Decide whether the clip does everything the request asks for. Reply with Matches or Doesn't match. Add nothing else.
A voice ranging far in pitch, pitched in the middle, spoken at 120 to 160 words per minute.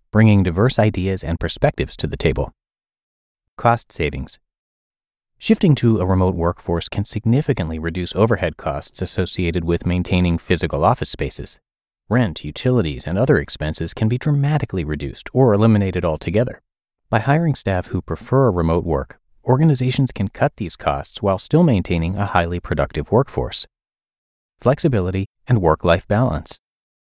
Doesn't match